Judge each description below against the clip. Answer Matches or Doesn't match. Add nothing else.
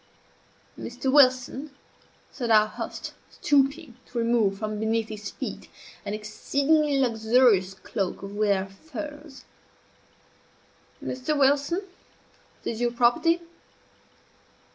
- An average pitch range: Matches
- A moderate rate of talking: Doesn't match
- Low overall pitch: Doesn't match